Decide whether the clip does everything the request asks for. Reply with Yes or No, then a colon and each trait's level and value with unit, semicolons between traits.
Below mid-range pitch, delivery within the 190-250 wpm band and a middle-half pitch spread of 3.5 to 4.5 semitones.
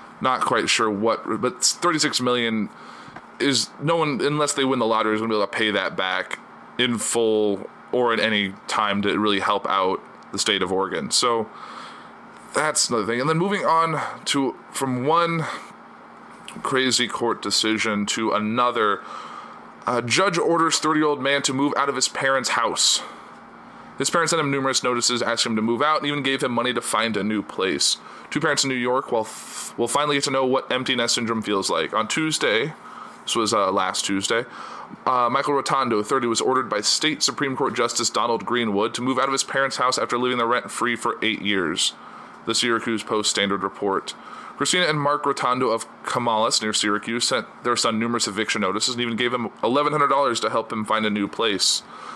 Yes: low, 125 Hz; average, 195 wpm; average, 4.0 semitones